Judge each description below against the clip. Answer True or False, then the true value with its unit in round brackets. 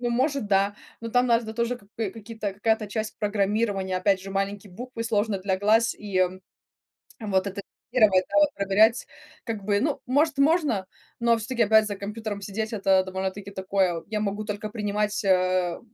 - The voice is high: True (210 Hz)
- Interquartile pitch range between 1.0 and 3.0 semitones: True (2.6 semitones)